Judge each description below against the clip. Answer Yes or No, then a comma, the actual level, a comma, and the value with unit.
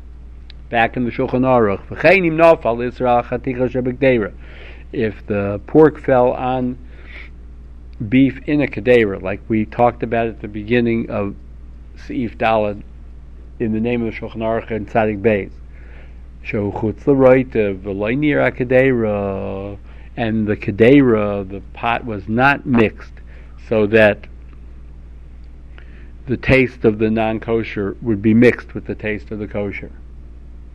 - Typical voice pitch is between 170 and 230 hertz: No, low, 105 Hz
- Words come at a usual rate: No, slow, 115 wpm